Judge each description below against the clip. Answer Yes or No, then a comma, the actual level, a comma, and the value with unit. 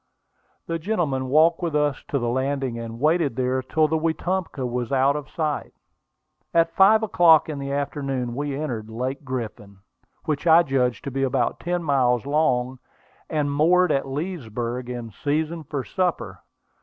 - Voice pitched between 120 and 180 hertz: Yes, medium, 140 Hz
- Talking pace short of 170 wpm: Yes, average, 160 wpm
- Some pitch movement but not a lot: Yes, average, 3.9 semitones